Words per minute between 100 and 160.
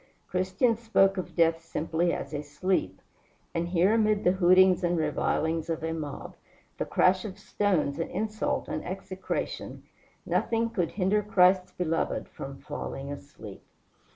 Yes: average, 145 wpm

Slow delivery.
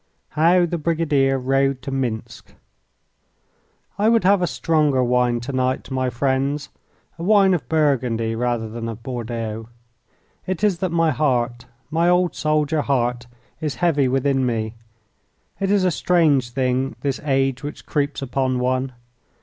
No: average, 150 wpm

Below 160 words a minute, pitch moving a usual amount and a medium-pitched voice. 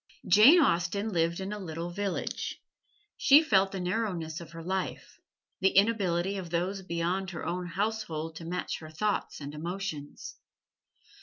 Yes: average, 150 wpm; average, 3.0 semitones; medium, 180 Hz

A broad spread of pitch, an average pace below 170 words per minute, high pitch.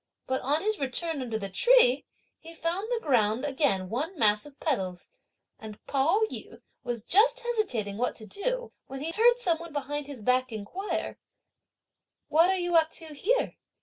No: wide, 7.7 semitones; average, 175 wpm; very high, 295 Hz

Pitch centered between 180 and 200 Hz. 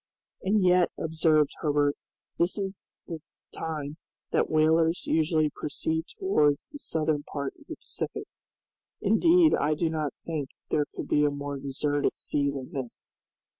No: medium, 155 Hz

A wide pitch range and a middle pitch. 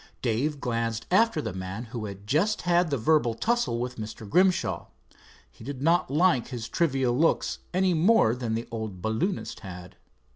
No: wide, 7.3 semitones; low, 125 Hz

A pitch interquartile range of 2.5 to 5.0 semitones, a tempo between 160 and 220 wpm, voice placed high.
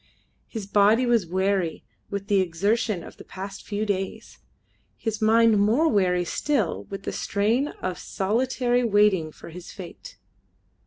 No: average, 3.3 semitones; average, 145 wpm; high, 200 Hz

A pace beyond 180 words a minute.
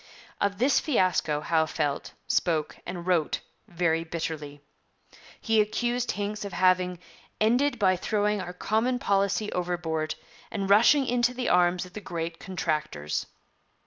No: slow, 135 wpm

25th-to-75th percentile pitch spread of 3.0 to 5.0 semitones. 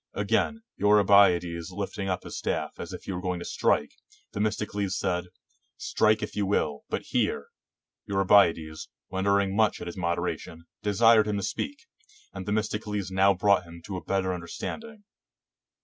No: narrow, 2.6 semitones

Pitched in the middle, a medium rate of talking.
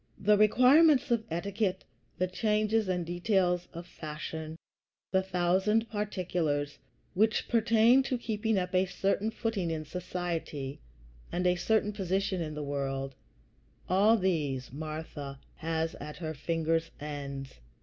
No: medium, 180 Hz; slow, 130 wpm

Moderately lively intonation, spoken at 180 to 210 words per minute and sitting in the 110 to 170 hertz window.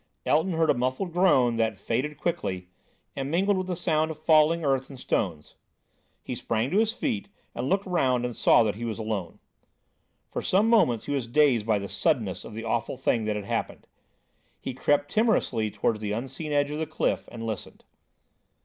No: wide, 6.4 semitones; average, 195 wpm; low, 135 Hz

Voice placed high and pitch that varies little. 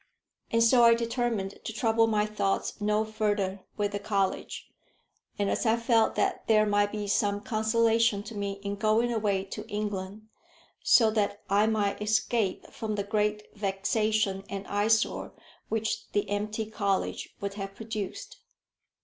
Yes: high, 210 Hz; narrow, 1.6 semitones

